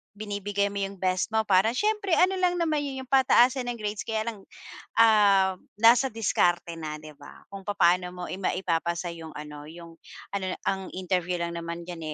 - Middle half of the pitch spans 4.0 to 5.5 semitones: Yes, average, 4.7 semitones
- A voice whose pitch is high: Yes, high, 195 Hz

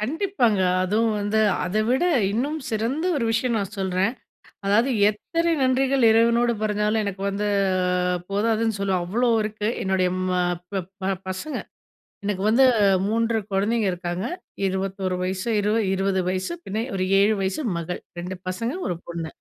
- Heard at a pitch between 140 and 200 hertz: No, high, 210 Hz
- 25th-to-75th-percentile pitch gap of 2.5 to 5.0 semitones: Yes, average, 3.5 semitones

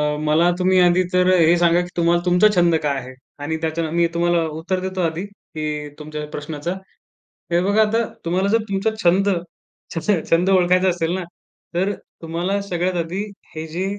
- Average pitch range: No, narrow, 2.3 semitones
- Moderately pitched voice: Yes, medium, 175 Hz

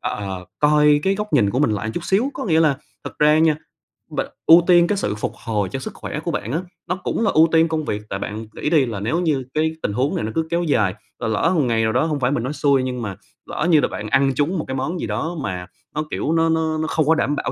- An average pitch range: No, wide, 6.1 semitones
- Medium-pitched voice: Yes, medium, 150 Hz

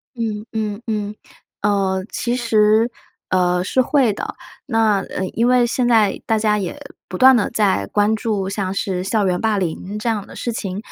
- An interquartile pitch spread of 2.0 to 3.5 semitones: Yes, average, 2.8 semitones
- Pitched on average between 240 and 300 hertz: No, high, 210 Hz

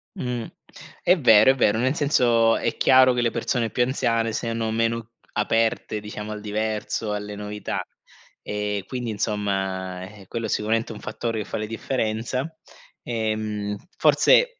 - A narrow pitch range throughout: Yes, narrow, 2.2 semitones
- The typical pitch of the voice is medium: No, low, 110 Hz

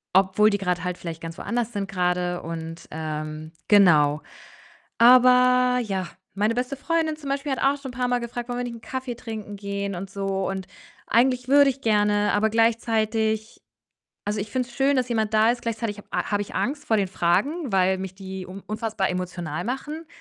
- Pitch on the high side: Yes, high, 215 Hz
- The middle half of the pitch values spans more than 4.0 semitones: Yes, average, 4.6 semitones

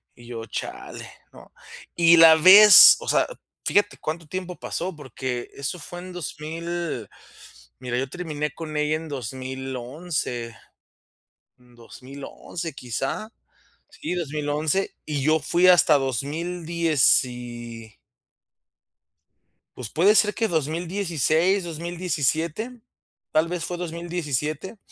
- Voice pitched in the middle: Yes, medium, 155 Hz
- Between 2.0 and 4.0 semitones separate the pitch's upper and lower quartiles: No, average, 4.6 semitones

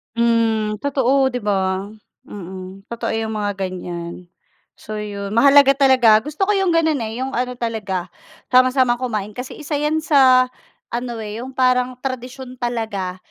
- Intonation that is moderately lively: Yes, average, 3.8 semitones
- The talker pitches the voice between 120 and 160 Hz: No, high, 235 Hz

